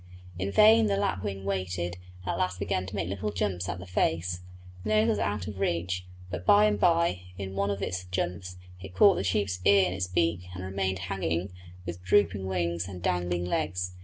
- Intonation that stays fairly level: Yes, narrow, 1.8 semitones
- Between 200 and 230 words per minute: Yes, fast, 205 wpm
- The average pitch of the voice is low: Yes, very low, 95 Hz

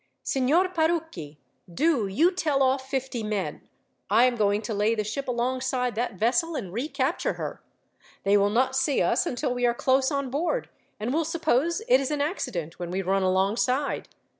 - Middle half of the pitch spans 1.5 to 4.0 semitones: No, wide, 5.4 semitones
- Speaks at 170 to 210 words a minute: Yes, average, 180 wpm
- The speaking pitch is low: No, very high, 255 Hz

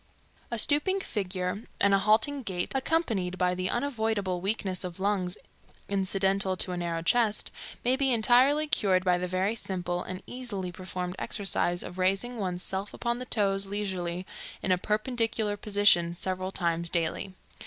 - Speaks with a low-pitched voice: No, high, 195 Hz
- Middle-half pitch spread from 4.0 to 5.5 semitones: No, average, 3.4 semitones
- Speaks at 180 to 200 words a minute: No, average, 155 wpm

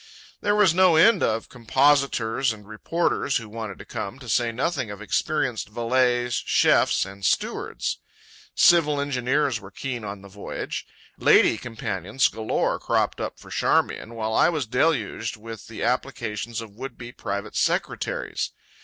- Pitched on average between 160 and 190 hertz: No, low, 120 Hz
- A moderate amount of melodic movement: Yes, average, 3.9 semitones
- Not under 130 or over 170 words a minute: Yes, average, 150 wpm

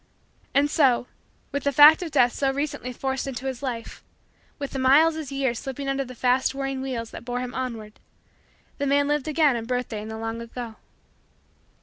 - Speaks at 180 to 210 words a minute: Yes, average, 195 wpm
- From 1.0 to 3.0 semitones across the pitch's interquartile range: Yes, narrow, 2.6 semitones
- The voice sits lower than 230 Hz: No, very high, 265 Hz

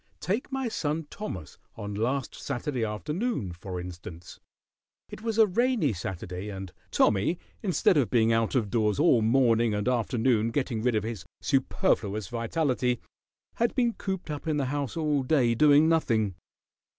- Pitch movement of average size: No, wide, 6.6 semitones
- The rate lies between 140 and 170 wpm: Yes, average, 155 wpm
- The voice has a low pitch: Yes, low, 125 Hz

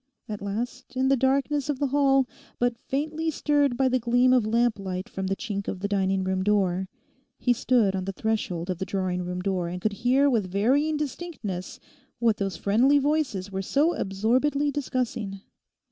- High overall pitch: Yes, high, 230 Hz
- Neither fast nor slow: Yes, average, 180 wpm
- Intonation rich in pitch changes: Yes, wide, 5.8 semitones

